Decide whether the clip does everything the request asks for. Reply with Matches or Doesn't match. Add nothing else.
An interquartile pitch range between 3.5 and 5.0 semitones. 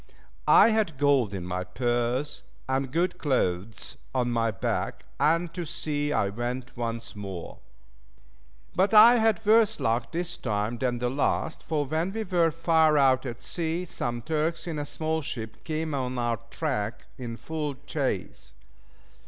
Doesn't match